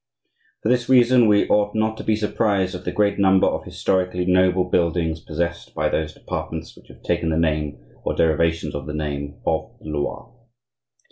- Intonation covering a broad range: No, average, 4.5 semitones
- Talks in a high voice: No, very low, 90 Hz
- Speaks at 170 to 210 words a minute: Yes, average, 185 wpm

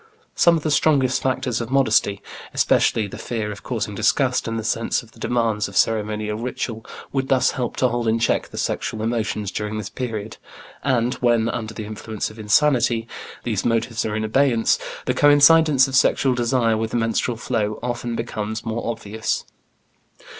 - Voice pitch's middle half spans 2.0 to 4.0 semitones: Yes, narrow, 2.6 semitones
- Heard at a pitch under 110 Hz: No, low, 115 Hz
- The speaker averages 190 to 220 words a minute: No, average, 175 wpm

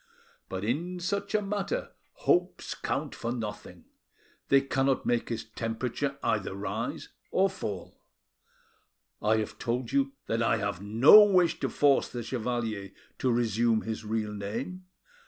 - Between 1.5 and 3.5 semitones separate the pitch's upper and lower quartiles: No, average, 4.8 semitones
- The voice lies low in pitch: Yes, low, 120 Hz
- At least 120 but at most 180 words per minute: Yes, slow, 135 wpm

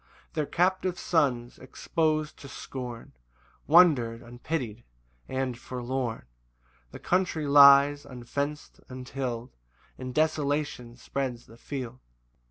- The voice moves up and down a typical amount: Yes, average, 3.6 semitones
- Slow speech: Yes, slow, 100 wpm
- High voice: No, low, 135 Hz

